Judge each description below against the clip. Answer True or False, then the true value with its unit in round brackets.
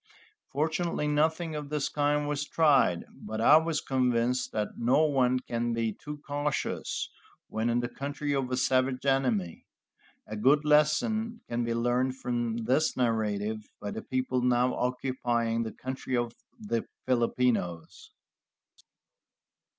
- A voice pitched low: True (130 Hz)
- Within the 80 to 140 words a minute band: True (135 wpm)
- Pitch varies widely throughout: False (3.9 semitones)